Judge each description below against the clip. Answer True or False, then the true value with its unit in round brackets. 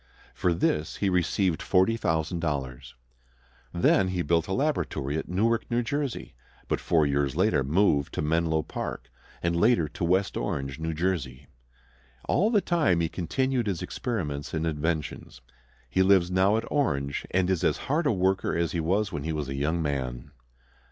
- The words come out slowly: False (160 wpm)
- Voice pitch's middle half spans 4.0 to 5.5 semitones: True (4.5 semitones)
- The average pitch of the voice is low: True (85 Hz)